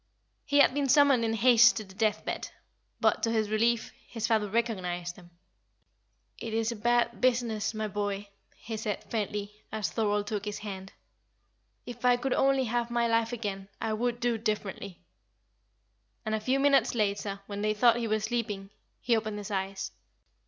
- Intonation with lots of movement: No, narrow, 2.4 semitones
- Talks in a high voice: Yes, high, 220 Hz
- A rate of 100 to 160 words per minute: No, average, 175 wpm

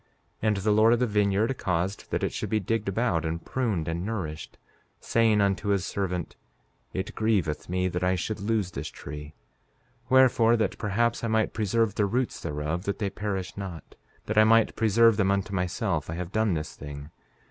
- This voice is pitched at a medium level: No, low, 100 Hz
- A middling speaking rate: Yes, average, 190 wpm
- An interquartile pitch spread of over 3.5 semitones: Yes, average, 3.9 semitones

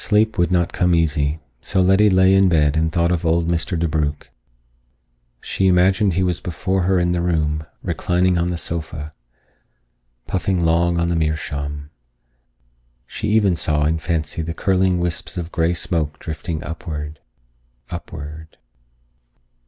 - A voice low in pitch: Yes, very low, 85 Hz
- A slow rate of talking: No, average, 145 wpm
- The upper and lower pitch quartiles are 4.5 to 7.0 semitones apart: No, narrow, 2.4 semitones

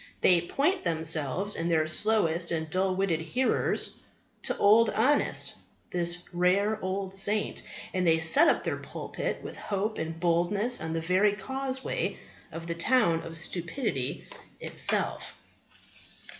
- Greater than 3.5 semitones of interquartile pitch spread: Yes, average, 4.2 semitones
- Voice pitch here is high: No, medium, 180 Hz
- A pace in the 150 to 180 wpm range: No, slow, 135 wpm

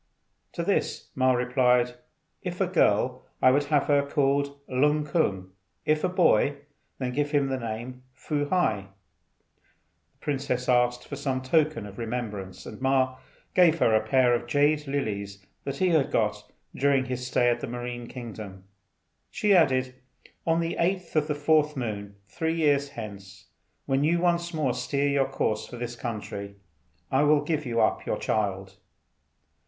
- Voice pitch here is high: No, low, 130 Hz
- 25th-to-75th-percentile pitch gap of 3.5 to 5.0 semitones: Yes, average, 3.9 semitones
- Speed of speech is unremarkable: Yes, average, 160 wpm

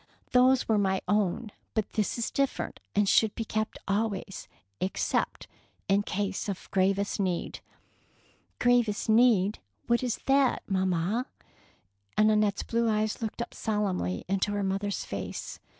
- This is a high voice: Yes, high, 210 Hz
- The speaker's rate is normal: Yes, average, 150 wpm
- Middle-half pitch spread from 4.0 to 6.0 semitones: No, average, 2.7 semitones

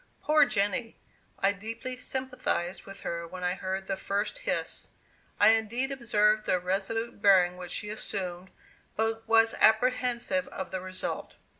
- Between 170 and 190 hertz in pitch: No, high, 210 Hz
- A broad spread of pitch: No, average, 3.7 semitones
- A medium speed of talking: Yes, average, 145 wpm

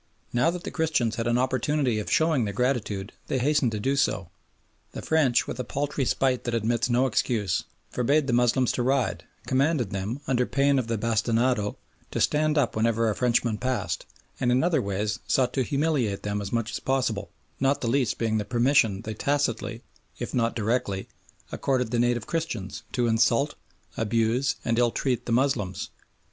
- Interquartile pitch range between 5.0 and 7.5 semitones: No, average, 3.2 semitones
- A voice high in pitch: No, low, 120 Hz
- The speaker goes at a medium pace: Yes, average, 180 wpm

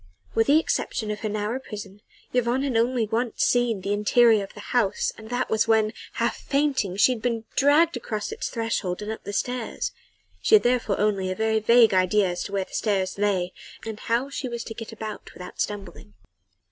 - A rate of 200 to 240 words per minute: Yes, fast, 205 wpm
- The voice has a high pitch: Yes, high, 220 Hz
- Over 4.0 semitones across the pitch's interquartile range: No, average, 3.0 semitones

